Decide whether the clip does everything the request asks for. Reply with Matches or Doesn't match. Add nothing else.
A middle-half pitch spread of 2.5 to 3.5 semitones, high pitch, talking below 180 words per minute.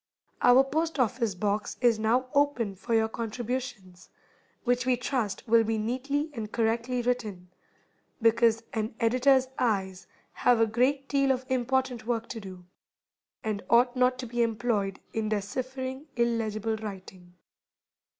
Matches